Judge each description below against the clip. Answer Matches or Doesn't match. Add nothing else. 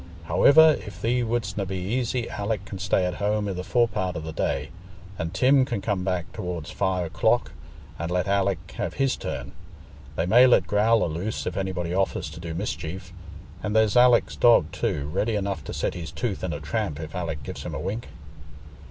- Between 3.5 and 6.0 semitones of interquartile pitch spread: Matches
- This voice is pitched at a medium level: Doesn't match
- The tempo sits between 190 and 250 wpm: Matches